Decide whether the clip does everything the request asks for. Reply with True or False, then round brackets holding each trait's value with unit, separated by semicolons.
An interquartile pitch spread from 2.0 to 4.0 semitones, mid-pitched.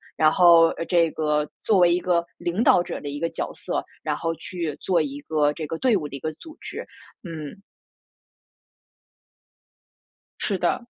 True (2.7 semitones; 165 Hz)